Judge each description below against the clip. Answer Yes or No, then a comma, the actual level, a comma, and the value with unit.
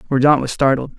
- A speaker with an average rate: Yes, average, 185 wpm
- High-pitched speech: No, low, 135 Hz